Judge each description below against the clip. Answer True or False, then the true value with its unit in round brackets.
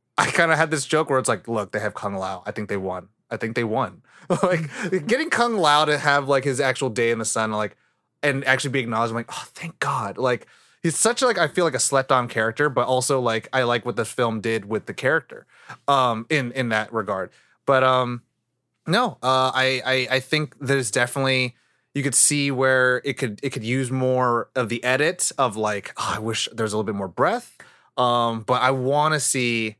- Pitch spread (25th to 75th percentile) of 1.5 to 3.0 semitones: False (3.4 semitones)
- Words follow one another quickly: True (230 wpm)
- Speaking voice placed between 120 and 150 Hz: True (130 Hz)